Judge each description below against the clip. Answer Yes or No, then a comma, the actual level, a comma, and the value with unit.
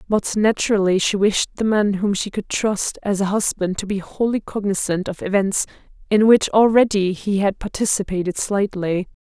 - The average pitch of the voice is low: No, high, 200 Hz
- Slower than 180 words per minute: Yes, average, 170 wpm